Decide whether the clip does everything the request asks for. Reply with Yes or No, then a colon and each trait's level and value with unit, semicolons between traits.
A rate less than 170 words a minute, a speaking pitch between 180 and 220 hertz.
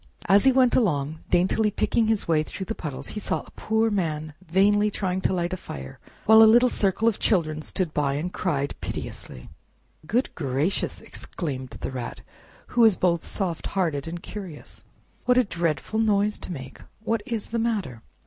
No: average, 180 wpm; medium, 185 Hz